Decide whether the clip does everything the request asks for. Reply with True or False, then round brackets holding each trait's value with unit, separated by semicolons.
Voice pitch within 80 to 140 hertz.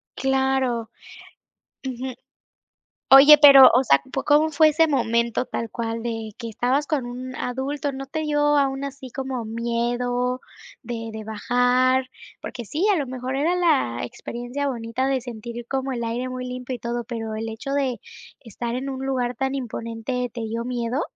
False (250 Hz)